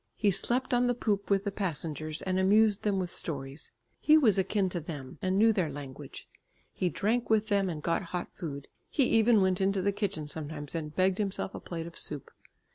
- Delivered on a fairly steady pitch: No, average, 4.5 semitones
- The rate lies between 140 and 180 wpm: No, fast, 205 wpm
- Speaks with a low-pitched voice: No, high, 190 Hz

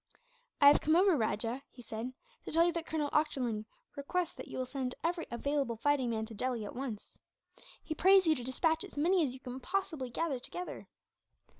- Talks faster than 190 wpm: Yes, average, 200 wpm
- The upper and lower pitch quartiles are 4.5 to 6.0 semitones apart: Yes, average, 4.9 semitones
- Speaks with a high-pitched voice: Yes, very high, 280 Hz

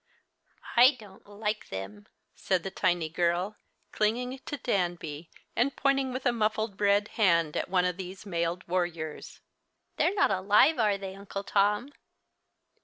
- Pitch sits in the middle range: No, high, 195 Hz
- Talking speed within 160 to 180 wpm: No, average, 145 wpm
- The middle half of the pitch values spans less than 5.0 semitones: Yes, average, 3.8 semitones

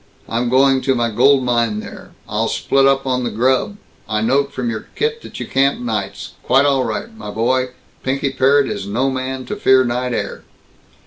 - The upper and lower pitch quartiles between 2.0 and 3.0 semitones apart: Yes, narrow, 2.4 semitones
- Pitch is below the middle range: Yes, low, 130 Hz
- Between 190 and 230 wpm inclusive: Yes, average, 195 wpm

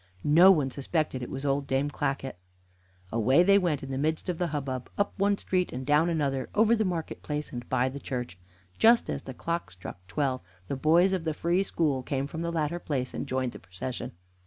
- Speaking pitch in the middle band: Yes, medium, 145 Hz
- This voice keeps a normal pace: No, fast, 215 wpm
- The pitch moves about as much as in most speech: Yes, average, 4.4 semitones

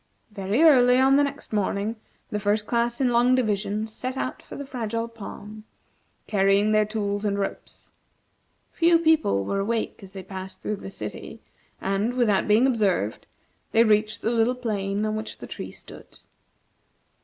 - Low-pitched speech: No, high, 215 Hz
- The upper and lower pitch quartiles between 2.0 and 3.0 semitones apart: No, average, 3.4 semitones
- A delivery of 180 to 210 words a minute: No, average, 165 wpm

